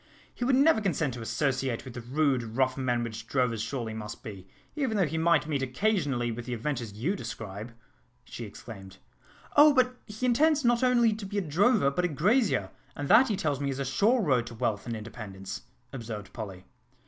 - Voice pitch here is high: No, low, 135 Hz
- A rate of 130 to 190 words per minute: No, average, 200 wpm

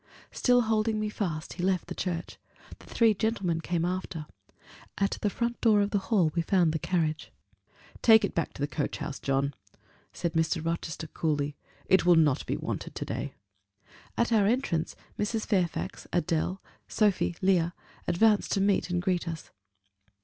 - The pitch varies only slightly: No, average, 4.2 semitones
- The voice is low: No, medium, 180 Hz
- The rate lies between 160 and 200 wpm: Yes, average, 170 wpm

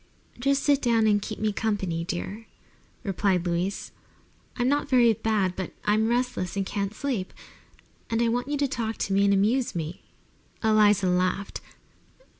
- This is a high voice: Yes, high, 215 Hz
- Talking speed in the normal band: Yes, average, 160 wpm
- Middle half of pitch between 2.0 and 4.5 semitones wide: Yes, average, 3.8 semitones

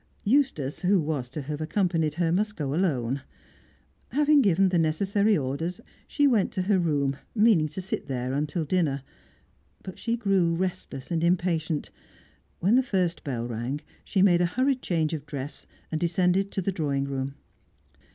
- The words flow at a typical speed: Yes, average, 165 wpm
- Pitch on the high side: No, medium, 170 Hz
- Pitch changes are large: No, average, 5.0 semitones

